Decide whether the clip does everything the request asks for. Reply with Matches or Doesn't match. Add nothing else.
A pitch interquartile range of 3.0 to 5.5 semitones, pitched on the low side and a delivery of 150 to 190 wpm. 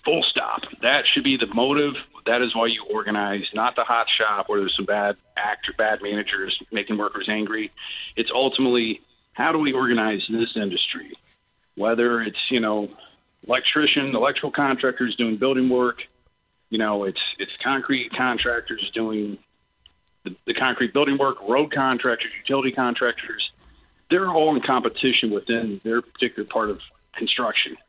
Matches